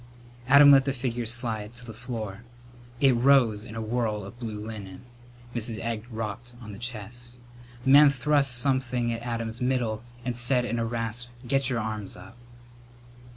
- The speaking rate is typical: Yes, average, 170 wpm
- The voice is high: No, low, 120 Hz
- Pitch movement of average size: No, narrow, 2.2 semitones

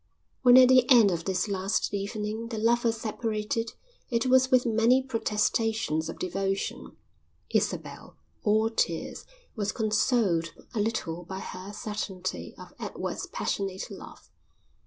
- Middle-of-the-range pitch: No, high, 215 Hz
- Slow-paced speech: Yes, slow, 130 wpm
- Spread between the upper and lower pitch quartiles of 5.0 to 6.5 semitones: No, average, 3.0 semitones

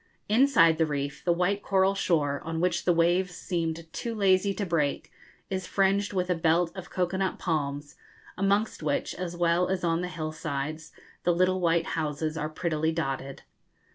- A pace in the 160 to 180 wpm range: Yes, average, 175 wpm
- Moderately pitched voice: Yes, medium, 170 Hz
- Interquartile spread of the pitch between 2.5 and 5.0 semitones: Yes, average, 2.8 semitones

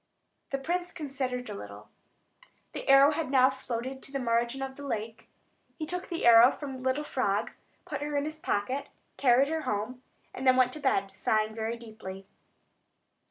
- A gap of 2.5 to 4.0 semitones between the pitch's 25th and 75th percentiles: Yes, average, 3.7 semitones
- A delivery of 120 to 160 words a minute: No, average, 180 wpm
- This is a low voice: No, very high, 260 Hz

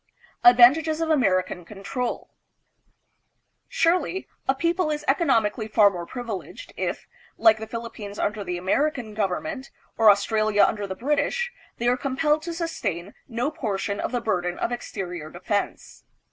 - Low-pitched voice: No, high, 230 Hz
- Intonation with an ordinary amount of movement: No, wide, 6.4 semitones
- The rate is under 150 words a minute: Yes, average, 140 wpm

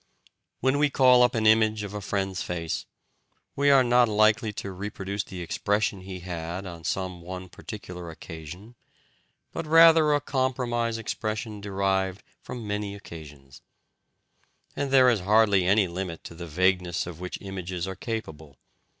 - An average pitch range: Yes, average, 4.0 semitones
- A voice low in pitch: Yes, low, 100 Hz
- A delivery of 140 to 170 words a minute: Yes, average, 150 wpm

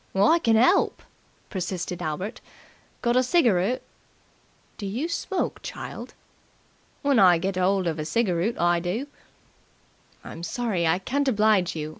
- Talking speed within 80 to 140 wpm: Yes, slow, 135 wpm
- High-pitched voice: Yes, high, 195 Hz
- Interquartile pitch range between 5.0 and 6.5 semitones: Yes, wide, 5.4 semitones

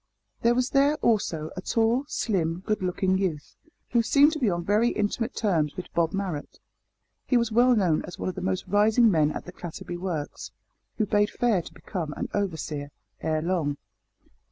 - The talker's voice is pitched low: No, high, 190 Hz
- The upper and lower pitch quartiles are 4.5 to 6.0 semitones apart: Yes, average, 5.2 semitones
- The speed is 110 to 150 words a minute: No, average, 185 wpm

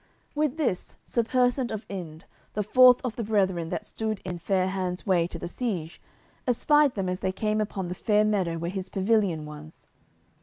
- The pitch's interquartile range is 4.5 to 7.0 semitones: No, average, 3.9 semitones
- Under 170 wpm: No, average, 190 wpm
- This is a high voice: Yes, high, 195 Hz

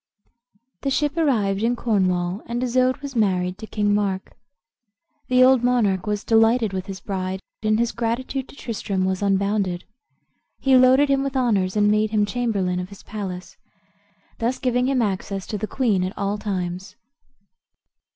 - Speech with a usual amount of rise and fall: Yes, average, 4.4 semitones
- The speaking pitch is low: No, high, 210 Hz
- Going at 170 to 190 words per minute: No, average, 160 wpm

